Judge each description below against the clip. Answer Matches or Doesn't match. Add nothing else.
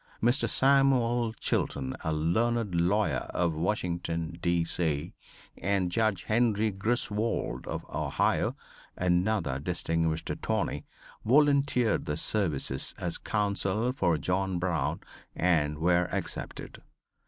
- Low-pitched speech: Matches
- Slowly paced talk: Matches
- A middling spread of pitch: Matches